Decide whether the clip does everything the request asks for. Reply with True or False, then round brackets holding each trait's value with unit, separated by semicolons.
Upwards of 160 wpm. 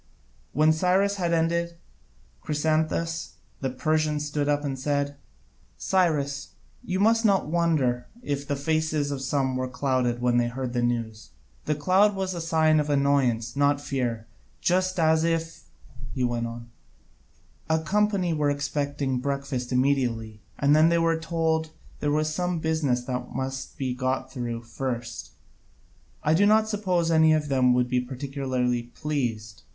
False (150 wpm)